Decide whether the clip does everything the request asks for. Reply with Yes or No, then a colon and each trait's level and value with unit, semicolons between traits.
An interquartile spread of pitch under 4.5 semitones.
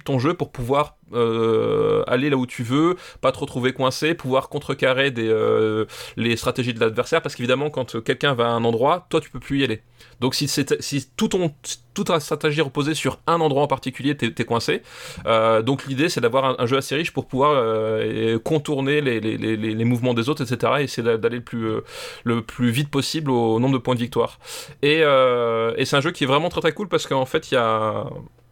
Yes: average, 4.0 semitones